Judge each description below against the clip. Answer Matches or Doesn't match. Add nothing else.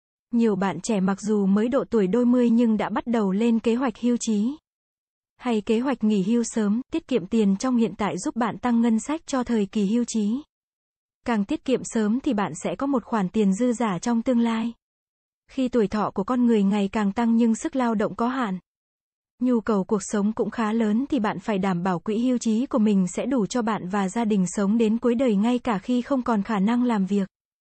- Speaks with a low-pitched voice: Doesn't match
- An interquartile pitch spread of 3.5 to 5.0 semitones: Doesn't match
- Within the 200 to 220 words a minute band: Doesn't match